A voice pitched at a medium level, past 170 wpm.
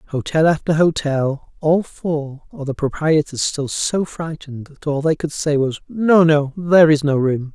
Yes: medium, 150 Hz; average, 185 wpm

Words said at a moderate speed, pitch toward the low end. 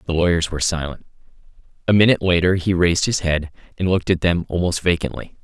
Yes: average, 190 wpm; very low, 85 Hz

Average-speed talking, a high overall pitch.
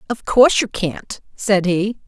Yes: average, 175 wpm; high, 205 Hz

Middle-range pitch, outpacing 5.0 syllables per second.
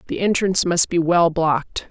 Yes: medium, 170 Hz; 5.2 syllables/s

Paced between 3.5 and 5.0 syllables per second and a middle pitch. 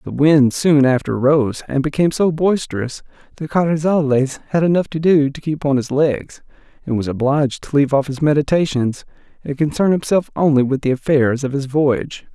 No: 5.3 syllables/s; medium, 145 Hz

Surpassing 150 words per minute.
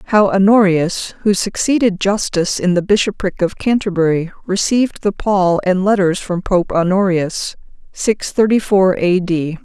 No: average, 145 wpm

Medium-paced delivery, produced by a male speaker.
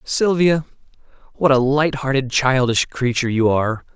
No: slow, 120 wpm; male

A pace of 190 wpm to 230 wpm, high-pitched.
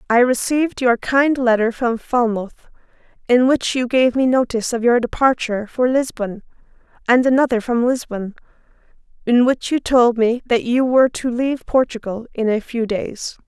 No: average, 165 wpm; high, 240 Hz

